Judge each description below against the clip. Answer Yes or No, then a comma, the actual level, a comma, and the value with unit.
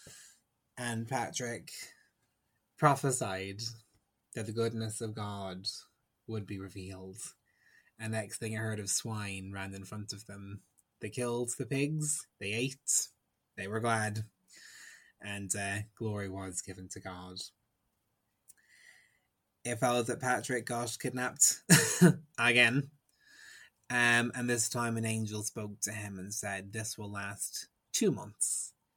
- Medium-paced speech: No, slow, 130 wpm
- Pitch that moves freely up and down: No, average, 3.3 semitones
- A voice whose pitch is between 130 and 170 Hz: No, low, 110 Hz